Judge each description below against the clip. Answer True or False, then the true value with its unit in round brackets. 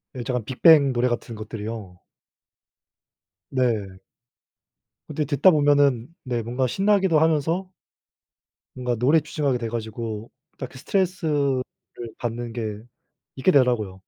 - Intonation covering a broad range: False (4.5 semitones)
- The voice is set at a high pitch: False (125 Hz)